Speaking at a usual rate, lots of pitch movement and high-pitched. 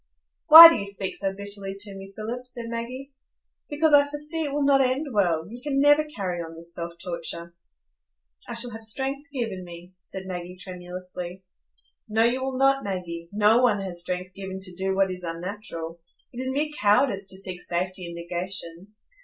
Yes: average, 185 wpm; wide, 5.9 semitones; high, 195 Hz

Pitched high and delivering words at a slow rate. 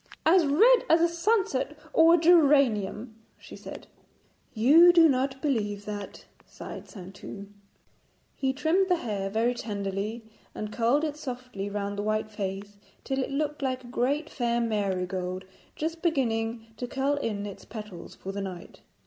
No: high, 240 Hz; average, 155 wpm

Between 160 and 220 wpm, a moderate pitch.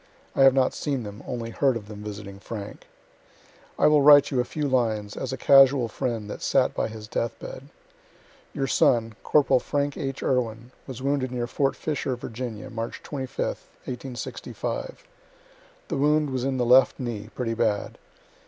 No: average, 170 wpm; low, 125 Hz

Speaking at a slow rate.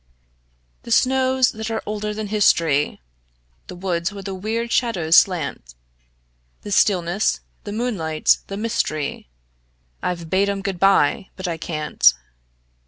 Yes: slow, 130 wpm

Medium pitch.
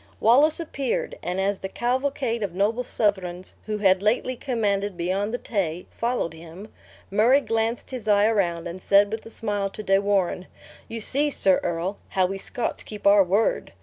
No: high, 205 Hz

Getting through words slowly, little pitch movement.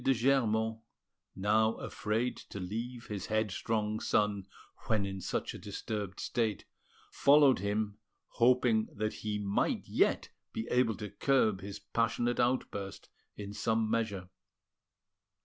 Yes: slow, 125 wpm; narrow, 2.3 semitones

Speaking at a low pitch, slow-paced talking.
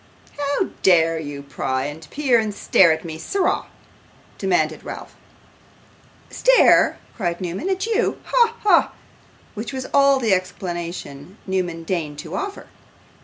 No: medium, 185 Hz; slow, 130 wpm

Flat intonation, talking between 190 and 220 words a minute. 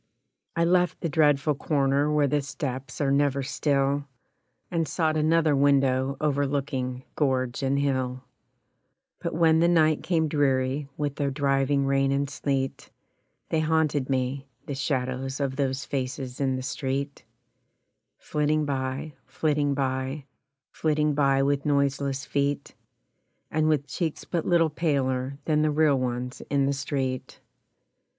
No: narrow, 2.0 semitones; slow, 135 wpm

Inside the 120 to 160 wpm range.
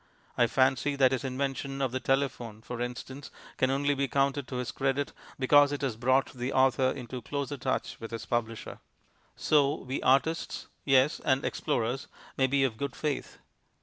No: average, 175 wpm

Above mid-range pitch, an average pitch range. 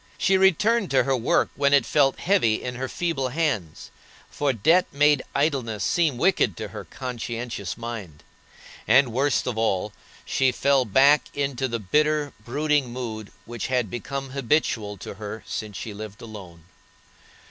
No: low, 130 Hz; average, 4.7 semitones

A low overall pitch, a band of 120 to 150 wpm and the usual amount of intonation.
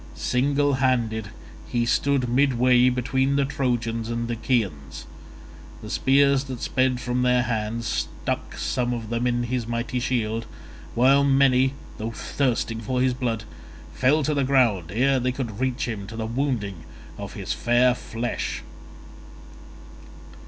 No: low, 125 Hz; average, 140 wpm; narrow, 2.3 semitones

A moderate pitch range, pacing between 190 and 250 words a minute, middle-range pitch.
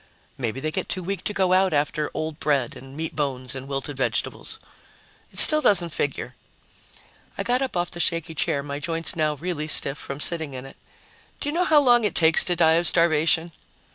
Yes: average, 3.9 semitones; fast, 205 wpm; medium, 160 Hz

